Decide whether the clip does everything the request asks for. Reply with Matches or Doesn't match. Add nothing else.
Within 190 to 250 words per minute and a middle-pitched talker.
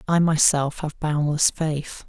Doesn't match